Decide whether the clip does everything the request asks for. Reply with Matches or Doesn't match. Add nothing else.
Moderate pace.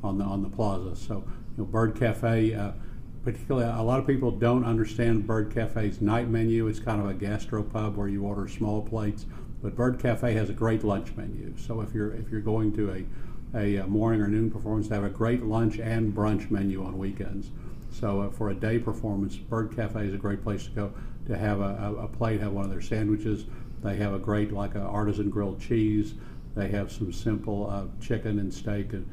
Doesn't match